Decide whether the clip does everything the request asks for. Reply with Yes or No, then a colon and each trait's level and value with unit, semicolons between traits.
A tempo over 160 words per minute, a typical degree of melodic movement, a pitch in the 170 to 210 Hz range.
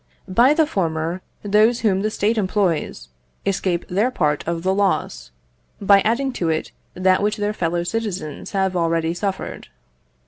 No: average, 150 wpm; average, 3.6 semitones; high, 190 Hz